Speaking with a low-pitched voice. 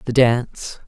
Yes: low, 120 Hz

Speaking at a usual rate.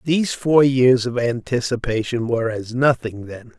Yes: average, 150 wpm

